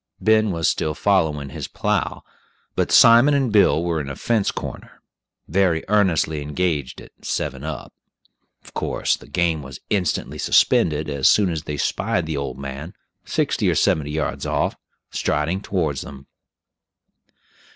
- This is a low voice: Yes, very low, 80 Hz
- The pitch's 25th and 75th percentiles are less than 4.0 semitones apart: No, average, 4.8 semitones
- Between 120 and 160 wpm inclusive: Yes, average, 150 wpm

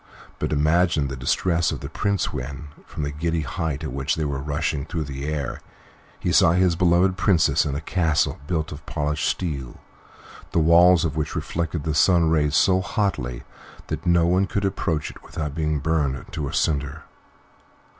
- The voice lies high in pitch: No, very low, 80 Hz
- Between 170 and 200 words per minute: Yes, average, 180 wpm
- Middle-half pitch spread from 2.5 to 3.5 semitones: Yes, average, 3.0 semitones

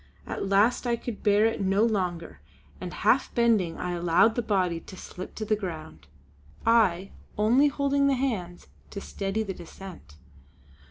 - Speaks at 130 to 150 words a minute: No, average, 160 wpm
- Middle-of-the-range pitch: No, high, 200 Hz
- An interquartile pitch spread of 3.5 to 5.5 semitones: Yes, average, 4.2 semitones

